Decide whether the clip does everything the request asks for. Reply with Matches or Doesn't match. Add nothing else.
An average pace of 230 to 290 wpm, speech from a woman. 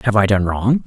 Doesn't match